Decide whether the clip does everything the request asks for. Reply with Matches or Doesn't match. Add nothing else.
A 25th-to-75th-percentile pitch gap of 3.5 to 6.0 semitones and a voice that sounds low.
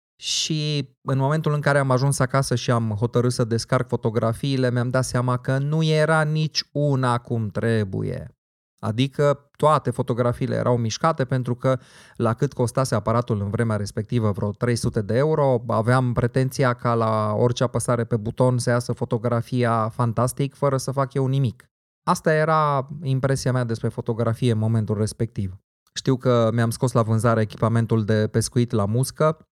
Doesn't match